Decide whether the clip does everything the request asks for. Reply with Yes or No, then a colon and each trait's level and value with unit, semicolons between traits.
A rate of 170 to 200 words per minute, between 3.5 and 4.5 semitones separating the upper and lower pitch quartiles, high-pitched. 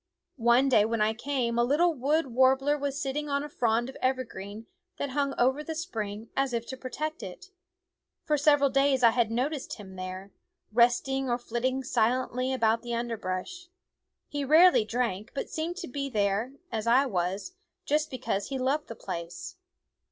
Yes: average, 175 wpm; average, 3.9 semitones; very high, 255 Hz